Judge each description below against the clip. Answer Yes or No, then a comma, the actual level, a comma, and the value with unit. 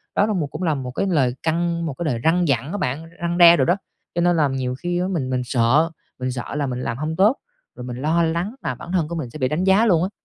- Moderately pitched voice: Yes, medium, 160 Hz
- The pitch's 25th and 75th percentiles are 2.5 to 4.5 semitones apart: No, average, 5.1 semitones